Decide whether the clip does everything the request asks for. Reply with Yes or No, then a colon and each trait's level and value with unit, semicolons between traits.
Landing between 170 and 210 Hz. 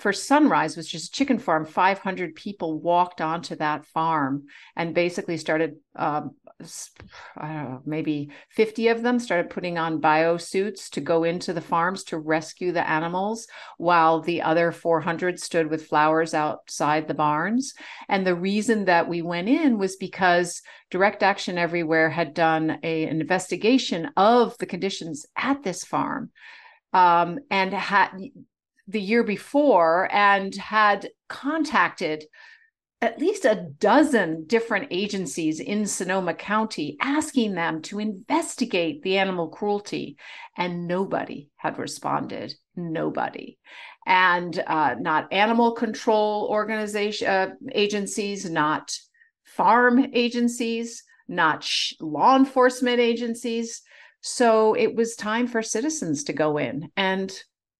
Yes: high, 190 Hz